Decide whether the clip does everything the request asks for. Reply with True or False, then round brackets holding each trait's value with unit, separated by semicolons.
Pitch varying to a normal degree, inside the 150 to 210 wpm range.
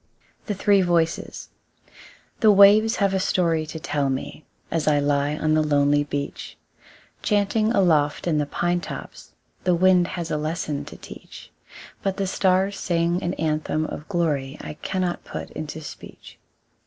True (3.9 semitones; 155 wpm)